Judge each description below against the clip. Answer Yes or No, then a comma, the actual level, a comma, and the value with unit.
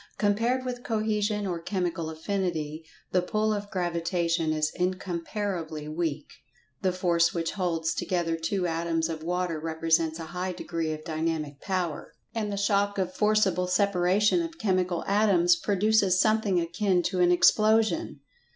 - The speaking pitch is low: No, medium, 180 Hz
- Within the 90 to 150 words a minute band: Yes, average, 140 wpm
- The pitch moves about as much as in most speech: Yes, average, 3.5 semitones